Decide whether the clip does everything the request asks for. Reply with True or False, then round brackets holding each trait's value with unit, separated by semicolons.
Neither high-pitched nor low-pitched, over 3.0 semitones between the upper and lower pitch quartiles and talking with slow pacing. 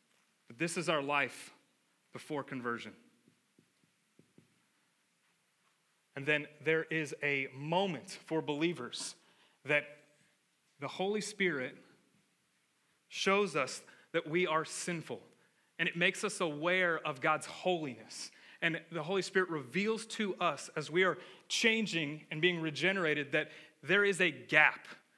True (160 Hz; 3.6 semitones; 120 wpm)